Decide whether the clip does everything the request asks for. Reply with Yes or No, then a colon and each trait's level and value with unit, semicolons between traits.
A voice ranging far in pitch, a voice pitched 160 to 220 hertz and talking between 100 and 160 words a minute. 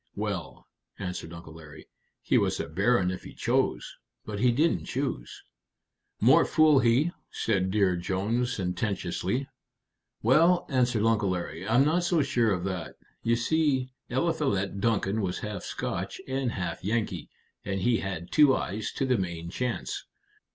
No: wide, 5.8 semitones; low, 110 Hz; average, 150 wpm